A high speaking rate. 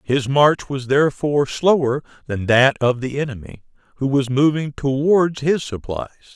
No: average, 150 wpm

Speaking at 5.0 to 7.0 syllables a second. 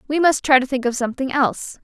Yes: 6.6 syllables/s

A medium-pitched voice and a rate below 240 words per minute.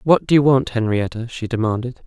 No: low, 120 Hz; fast, 205 wpm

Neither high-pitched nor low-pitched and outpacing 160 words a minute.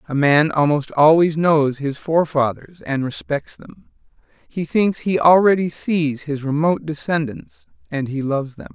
No: medium, 155 Hz; average, 150 wpm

